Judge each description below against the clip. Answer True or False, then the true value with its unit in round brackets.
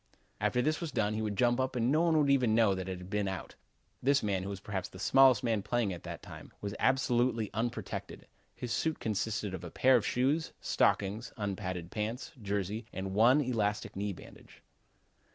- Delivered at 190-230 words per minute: True (200 wpm)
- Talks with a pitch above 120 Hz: False (110 Hz)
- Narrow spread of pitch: False (4.1 semitones)